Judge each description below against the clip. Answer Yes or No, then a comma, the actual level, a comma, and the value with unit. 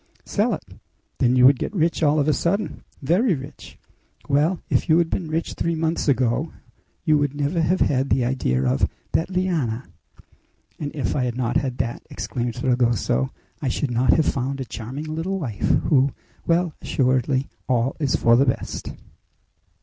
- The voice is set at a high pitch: No, medium, 140 Hz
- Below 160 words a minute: No, average, 175 wpm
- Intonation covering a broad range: No, average, 4.3 semitones